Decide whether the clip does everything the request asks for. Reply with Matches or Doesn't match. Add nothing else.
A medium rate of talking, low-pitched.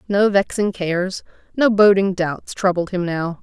Doesn't match